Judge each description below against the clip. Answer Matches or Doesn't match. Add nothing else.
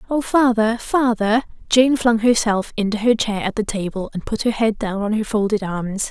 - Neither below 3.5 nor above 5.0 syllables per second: Matches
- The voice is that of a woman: Matches